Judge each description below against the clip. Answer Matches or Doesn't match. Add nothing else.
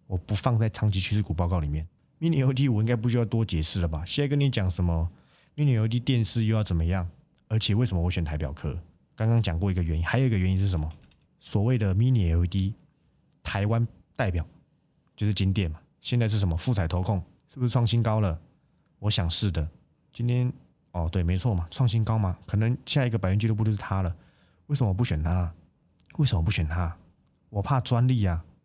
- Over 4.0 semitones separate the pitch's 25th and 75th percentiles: Matches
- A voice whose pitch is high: Doesn't match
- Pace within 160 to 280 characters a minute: Doesn't match